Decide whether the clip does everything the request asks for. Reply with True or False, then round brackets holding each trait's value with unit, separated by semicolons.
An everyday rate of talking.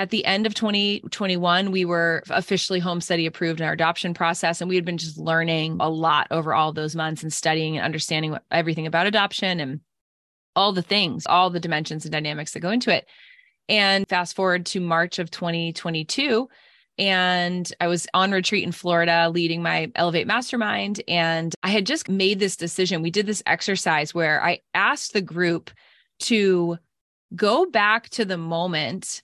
True (180 wpm)